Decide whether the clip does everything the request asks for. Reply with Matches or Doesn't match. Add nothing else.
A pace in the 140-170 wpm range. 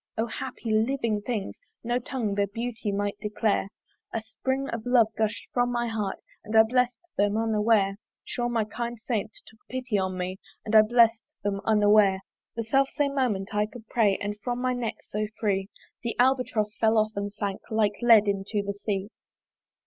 Doesn't match